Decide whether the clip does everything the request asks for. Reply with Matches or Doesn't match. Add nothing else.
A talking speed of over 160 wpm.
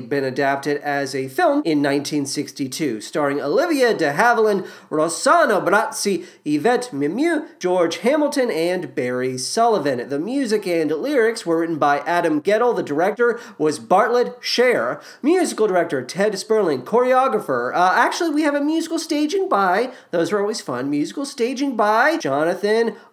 Doesn't match